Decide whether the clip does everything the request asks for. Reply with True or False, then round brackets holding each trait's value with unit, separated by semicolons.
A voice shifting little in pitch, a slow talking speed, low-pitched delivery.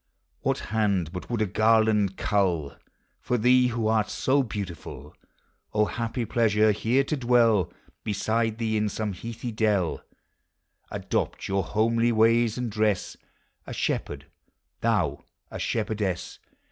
True (2.2 semitones; 130 wpm; 110 Hz)